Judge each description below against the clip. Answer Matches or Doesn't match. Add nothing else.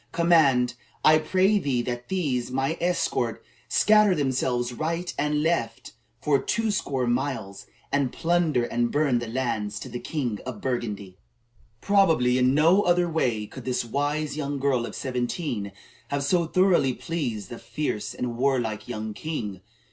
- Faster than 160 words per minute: Doesn't match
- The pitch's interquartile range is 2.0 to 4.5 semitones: Doesn't match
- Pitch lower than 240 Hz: Matches